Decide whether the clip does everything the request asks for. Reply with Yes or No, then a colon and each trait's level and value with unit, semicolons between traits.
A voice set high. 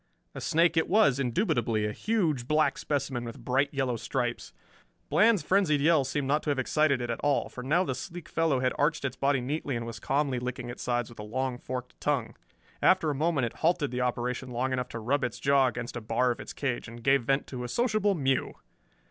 No: low, 135 Hz